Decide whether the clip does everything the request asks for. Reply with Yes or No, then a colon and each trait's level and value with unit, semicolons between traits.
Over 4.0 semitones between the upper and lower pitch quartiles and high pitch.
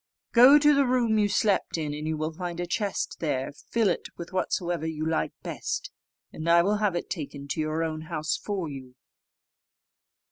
No: average, 4.8 semitones; medium, 170 Hz